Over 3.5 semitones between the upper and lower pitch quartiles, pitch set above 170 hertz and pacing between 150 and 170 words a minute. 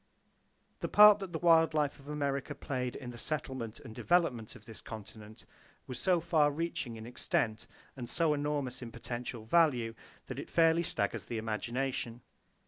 No: wide, 5.6 semitones; low, 130 Hz; average, 165 wpm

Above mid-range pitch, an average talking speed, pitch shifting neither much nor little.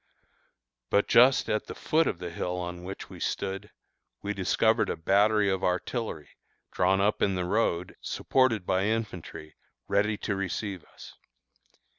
No: low, 100 Hz; average, 150 wpm; average, 3.0 semitones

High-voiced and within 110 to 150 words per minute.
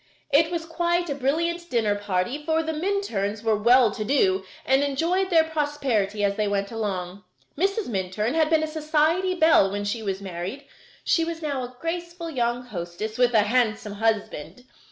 No: very high, 255 Hz; average, 175 wpm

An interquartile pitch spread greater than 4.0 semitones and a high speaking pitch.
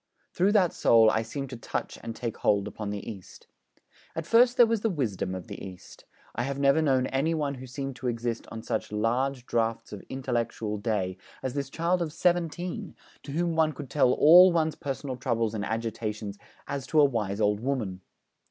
No: wide, 5.6 semitones; low, 130 Hz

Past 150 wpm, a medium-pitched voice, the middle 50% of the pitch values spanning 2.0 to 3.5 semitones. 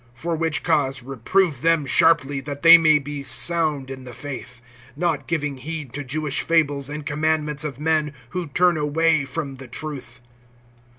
Yes: average, 165 wpm; medium, 150 Hz; average, 3.0 semitones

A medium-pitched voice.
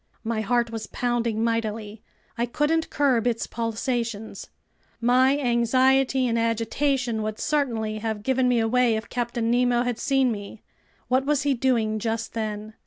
No: high, 235 Hz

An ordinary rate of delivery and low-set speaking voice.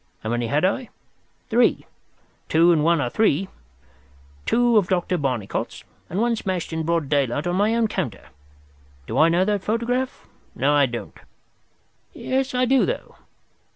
No: average, 150 wpm; medium, 170 Hz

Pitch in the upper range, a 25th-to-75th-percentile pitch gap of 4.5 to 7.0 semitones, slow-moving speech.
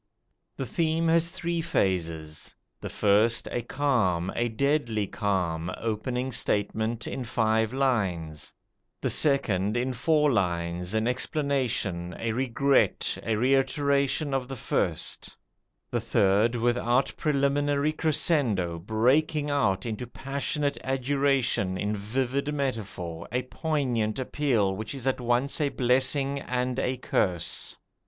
No: low, 125 Hz; average, 5.1 semitones; slow, 120 wpm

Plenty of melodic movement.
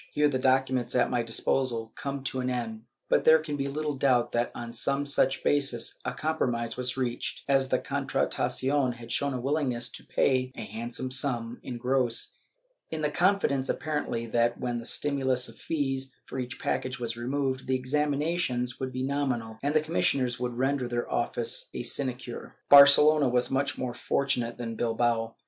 No: average, 2.7 semitones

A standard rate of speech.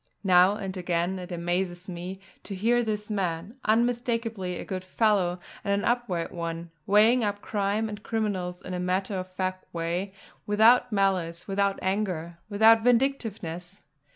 Yes: average, 150 wpm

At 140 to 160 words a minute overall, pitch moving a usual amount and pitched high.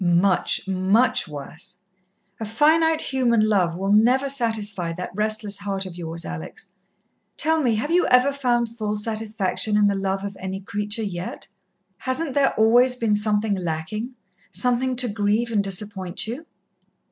Yes: average, 150 wpm; average, 4.1 semitones; high, 215 Hz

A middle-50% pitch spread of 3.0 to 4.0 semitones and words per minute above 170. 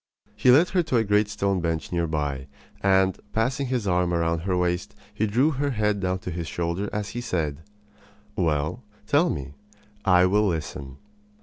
No: average, 4.8 semitones; average, 180 wpm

